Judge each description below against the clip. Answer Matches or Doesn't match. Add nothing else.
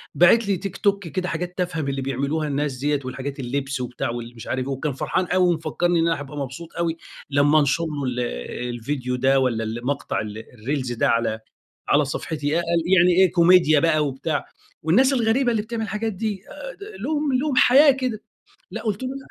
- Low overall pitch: Doesn't match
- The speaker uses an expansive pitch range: Matches